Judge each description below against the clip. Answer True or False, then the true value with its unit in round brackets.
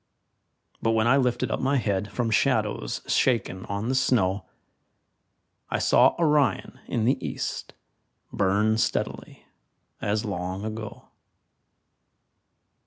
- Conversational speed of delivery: False (110 wpm)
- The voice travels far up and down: False (3.9 semitones)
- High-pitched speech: False (110 Hz)